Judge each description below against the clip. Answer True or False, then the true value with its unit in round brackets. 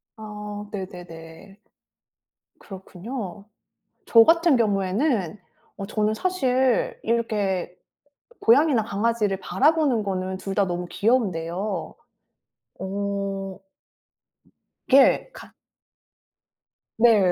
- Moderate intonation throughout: True (3.6 semitones)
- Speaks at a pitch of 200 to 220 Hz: True (205 Hz)